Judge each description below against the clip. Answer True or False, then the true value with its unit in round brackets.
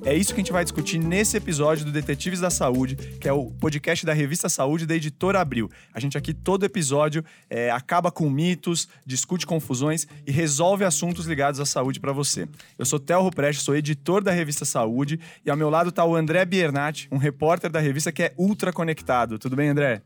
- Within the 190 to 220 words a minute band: True (205 wpm)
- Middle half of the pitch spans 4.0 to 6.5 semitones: False (3.4 semitones)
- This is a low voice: False (155 Hz)